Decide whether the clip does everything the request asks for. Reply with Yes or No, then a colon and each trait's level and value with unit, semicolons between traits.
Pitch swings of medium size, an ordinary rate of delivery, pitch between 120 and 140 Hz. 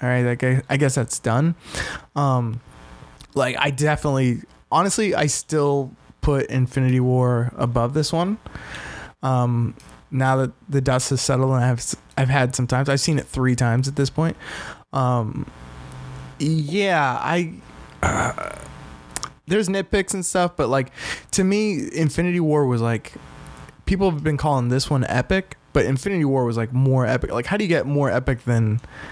Yes: average, 3.4 semitones; average, 165 wpm; low, 135 Hz